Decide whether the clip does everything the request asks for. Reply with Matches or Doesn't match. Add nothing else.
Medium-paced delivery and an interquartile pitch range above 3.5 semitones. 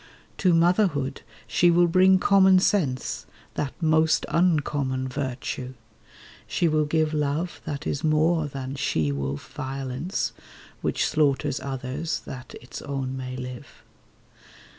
Doesn't match